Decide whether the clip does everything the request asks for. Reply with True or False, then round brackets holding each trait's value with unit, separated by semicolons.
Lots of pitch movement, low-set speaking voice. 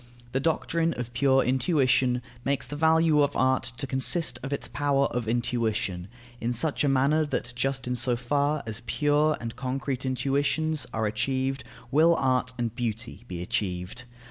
False (3.1 semitones; 130 Hz)